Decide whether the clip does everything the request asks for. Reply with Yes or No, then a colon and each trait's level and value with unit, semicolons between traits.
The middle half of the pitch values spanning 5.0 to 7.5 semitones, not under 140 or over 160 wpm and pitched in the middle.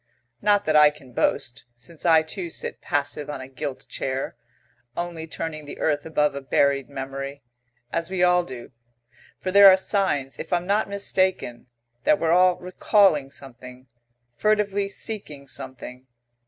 Yes: wide, 5.4 semitones; average, 155 wpm; medium, 155 Hz